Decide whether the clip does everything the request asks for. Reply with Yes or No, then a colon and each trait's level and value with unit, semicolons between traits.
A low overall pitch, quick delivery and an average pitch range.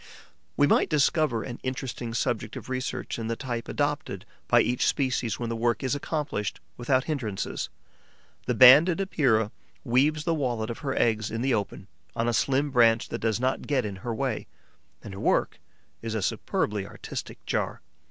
No: low, 120 Hz; average, 175 wpm; average, 3.5 semitones